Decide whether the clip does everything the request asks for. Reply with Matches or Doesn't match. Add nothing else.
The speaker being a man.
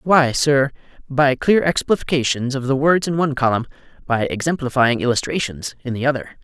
Matches